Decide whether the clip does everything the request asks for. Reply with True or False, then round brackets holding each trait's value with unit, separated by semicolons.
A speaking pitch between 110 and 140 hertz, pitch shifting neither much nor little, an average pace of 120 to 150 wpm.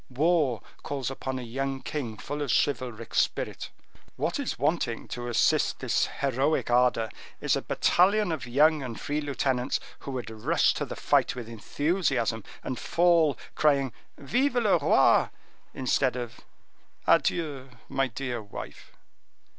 True (135 Hz; 3.8 semitones; 140 wpm)